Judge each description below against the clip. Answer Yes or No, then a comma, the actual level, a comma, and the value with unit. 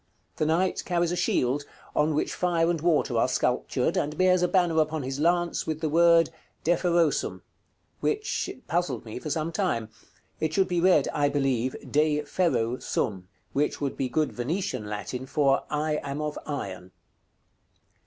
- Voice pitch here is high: No, medium, 150 Hz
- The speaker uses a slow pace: No, average, 165 wpm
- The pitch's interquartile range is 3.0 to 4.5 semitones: Yes, average, 4.1 semitones